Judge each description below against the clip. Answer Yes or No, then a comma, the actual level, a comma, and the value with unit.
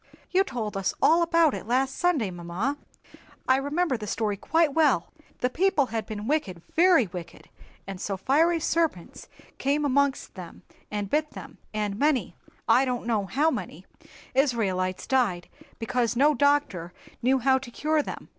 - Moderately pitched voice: No, very high, 260 Hz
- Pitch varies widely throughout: Yes, wide, 6.3 semitones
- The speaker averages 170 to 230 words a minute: No, average, 155 wpm